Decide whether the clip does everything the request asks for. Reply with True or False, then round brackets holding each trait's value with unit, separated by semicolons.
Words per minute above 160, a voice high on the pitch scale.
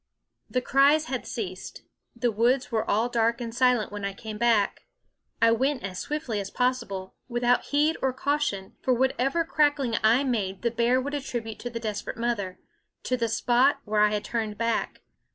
True (185 wpm; 235 Hz)